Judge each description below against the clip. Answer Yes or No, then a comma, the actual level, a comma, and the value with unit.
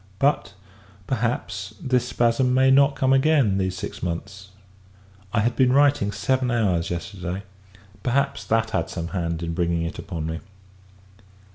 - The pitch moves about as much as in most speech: No, wide, 6.6 semitones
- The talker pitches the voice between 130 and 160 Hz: No, low, 110 Hz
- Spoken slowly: No, average, 145 wpm